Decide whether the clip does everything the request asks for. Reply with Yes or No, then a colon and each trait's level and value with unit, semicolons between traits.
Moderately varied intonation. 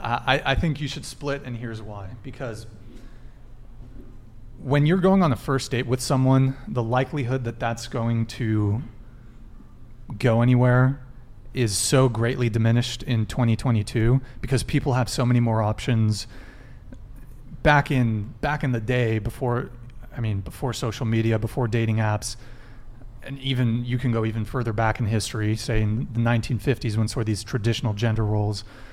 No: narrow, 2.3 semitones